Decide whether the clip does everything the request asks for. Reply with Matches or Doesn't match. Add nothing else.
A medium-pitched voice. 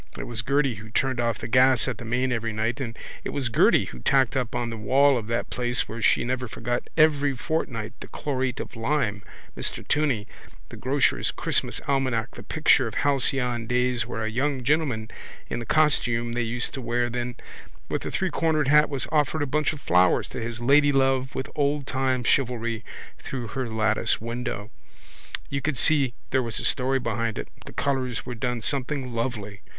Doesn't match